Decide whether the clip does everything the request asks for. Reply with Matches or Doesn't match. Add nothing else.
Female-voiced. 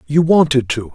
Doesn't match